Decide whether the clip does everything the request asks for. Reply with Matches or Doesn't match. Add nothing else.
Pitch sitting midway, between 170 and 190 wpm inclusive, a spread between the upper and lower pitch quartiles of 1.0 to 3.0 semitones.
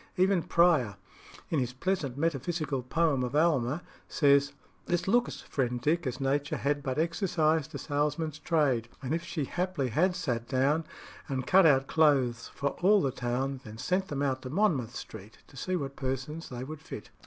Doesn't match